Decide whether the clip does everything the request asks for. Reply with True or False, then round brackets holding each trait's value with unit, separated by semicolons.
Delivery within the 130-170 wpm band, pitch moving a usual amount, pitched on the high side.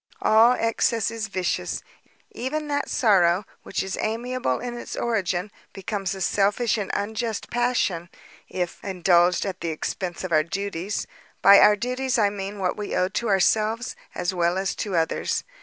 True (155 wpm; 3.9 semitones; 200 Hz)